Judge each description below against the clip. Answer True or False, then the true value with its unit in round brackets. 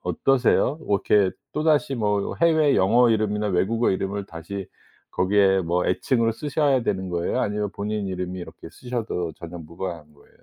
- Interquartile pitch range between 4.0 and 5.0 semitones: True (4.6 semitones)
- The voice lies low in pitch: True (100 Hz)